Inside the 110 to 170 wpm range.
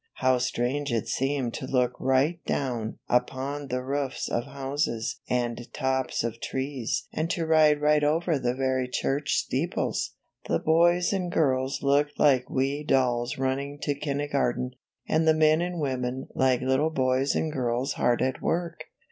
Yes: average, 155 wpm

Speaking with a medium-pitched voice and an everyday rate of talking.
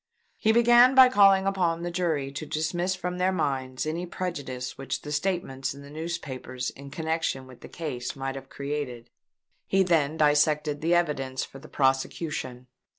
Yes: medium, 150 Hz; average, 165 wpm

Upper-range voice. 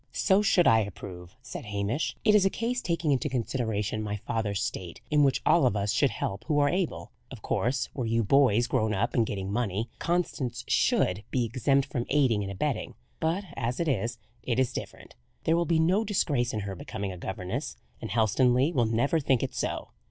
No: low, 120 Hz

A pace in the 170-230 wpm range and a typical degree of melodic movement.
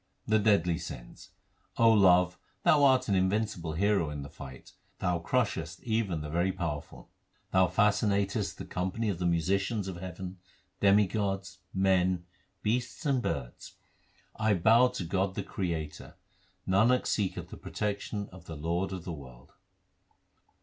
No: average, 145 wpm; average, 3.4 semitones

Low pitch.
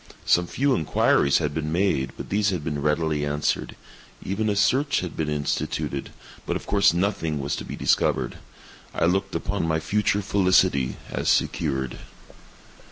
Yes: very low, 85 Hz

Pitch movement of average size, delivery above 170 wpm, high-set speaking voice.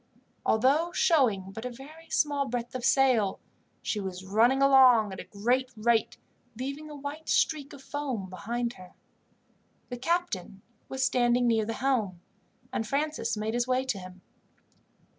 No: average, 4.2 semitones; average, 155 wpm; high, 245 Hz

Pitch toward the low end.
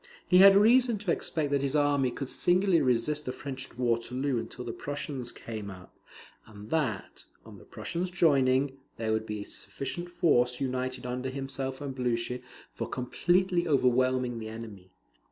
Yes: low, 130 Hz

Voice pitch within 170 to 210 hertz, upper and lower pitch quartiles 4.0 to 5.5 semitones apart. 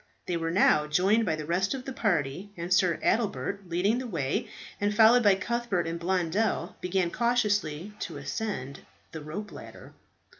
Yes: high, 190 Hz; average, 4.4 semitones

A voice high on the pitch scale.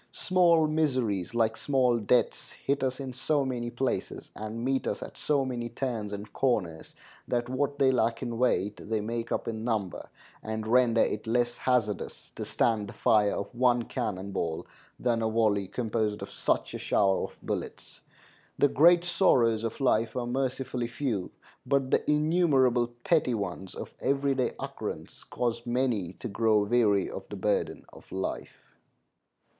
No: low, 120 Hz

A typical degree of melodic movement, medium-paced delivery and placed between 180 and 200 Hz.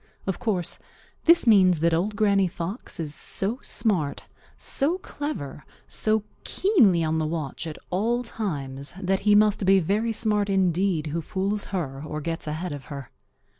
Yes: average, 5.0 semitones; average, 160 wpm; high, 190 Hz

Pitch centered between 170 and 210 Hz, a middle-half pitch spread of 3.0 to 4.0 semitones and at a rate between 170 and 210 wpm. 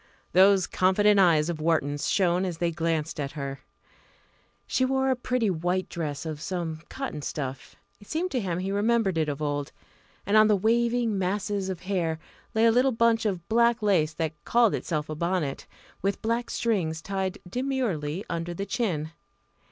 No: medium, 185 Hz; wide, 5.6 semitones; average, 175 wpm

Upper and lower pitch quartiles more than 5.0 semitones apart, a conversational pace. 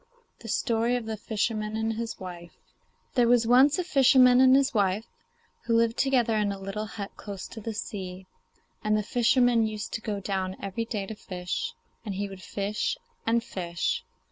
No: average, 3.2 semitones; average, 185 wpm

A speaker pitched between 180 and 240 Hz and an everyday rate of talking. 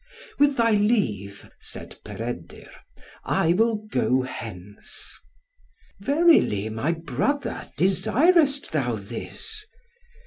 No: medium, 185 Hz; slow, 90 wpm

